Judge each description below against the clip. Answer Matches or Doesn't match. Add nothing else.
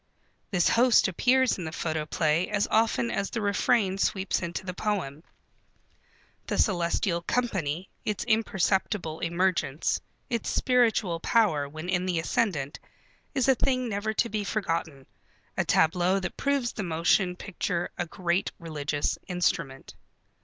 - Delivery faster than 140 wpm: Doesn't match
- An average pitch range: Matches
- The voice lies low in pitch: Doesn't match